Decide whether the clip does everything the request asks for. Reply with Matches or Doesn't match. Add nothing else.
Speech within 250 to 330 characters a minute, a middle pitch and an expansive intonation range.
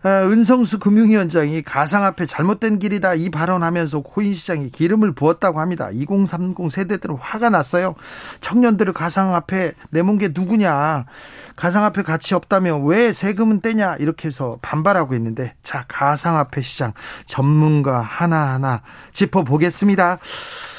Doesn't match